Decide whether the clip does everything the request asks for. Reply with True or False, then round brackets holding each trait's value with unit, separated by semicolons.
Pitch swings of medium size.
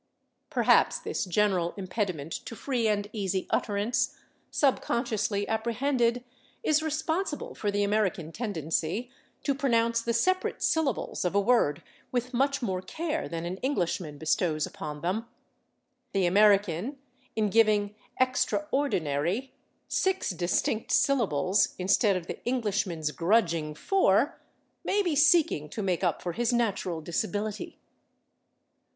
False (5.7 semitones)